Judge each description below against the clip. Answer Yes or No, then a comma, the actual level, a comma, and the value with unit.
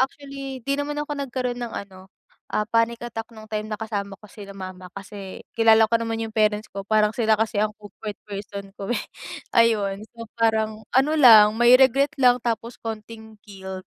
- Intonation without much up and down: Yes, narrow, 2.3 semitones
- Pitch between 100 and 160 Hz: No, high, 220 Hz